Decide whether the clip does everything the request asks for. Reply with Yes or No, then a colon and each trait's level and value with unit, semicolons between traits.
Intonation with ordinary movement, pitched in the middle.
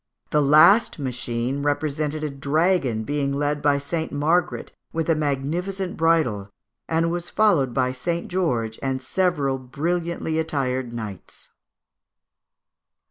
Yes: average, 4.0 semitones; medium, 145 Hz